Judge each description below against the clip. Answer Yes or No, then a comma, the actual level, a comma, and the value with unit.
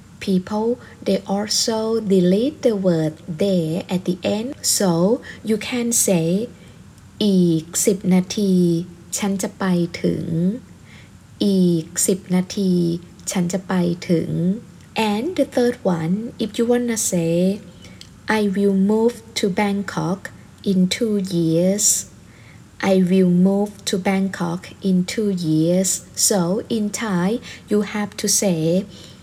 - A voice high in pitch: Yes, high, 195 Hz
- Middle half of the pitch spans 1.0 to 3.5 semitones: Yes, average, 3.1 semitones